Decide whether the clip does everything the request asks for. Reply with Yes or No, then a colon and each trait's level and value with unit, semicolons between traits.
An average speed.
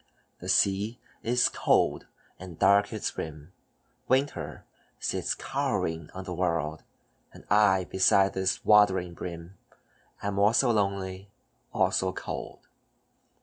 No: slow, 110 wpm